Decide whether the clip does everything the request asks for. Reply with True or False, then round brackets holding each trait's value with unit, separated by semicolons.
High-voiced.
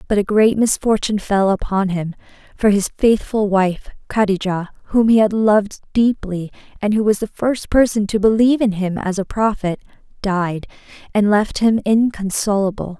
True (205 Hz)